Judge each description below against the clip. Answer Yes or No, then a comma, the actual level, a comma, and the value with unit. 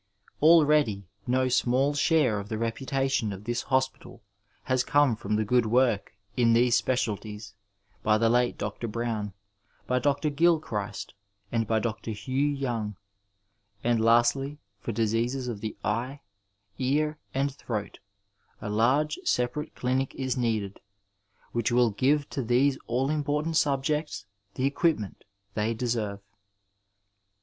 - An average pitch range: Yes, average, 3.8 semitones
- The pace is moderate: No, slow, 130 wpm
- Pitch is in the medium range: No, low, 125 Hz